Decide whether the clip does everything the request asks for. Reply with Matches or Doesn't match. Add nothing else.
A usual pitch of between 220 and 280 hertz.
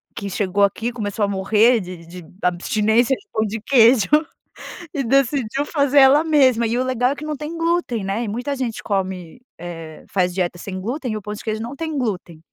Matches